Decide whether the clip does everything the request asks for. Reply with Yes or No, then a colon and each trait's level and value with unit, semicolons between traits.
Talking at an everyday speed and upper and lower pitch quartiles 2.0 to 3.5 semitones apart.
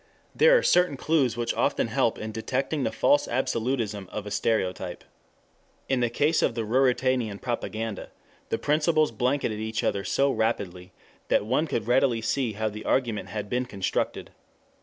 No: average, 160 wpm; average, 3.9 semitones